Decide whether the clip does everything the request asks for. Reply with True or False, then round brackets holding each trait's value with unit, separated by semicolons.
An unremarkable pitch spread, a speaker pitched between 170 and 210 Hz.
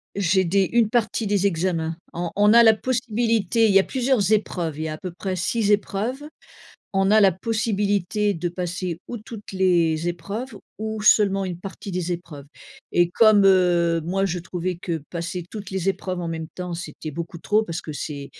True (3.5 semitones; 190 Hz)